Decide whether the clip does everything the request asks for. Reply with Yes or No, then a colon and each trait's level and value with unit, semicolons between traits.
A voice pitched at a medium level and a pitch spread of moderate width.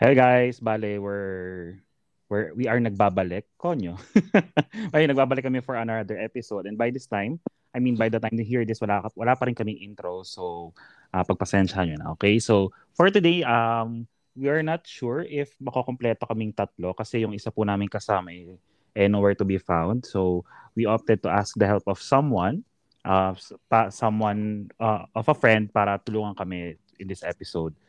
No: low, 110 Hz; average, 3.4 semitones